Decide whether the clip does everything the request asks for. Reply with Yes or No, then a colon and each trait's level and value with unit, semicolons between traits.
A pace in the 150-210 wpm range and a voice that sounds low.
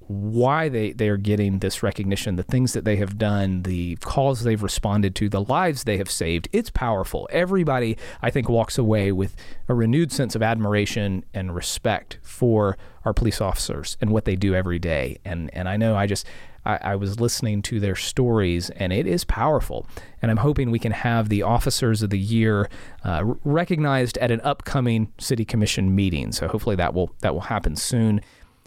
Yes: average, 195 wpm; low, 105 Hz